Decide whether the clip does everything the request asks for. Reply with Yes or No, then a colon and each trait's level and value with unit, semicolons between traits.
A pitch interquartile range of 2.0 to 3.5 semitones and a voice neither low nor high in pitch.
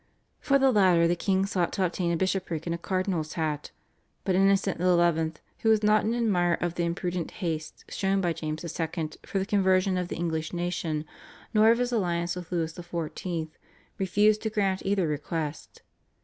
Yes: average, 2.7 semitones; medium, 175 Hz